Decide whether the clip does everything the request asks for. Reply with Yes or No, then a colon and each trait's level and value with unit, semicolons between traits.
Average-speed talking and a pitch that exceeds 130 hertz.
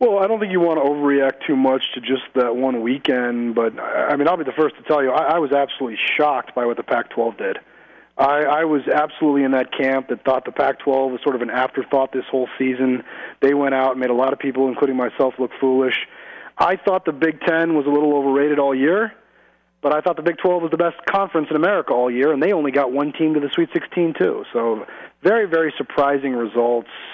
No: fast, 240 wpm; medium, 140 Hz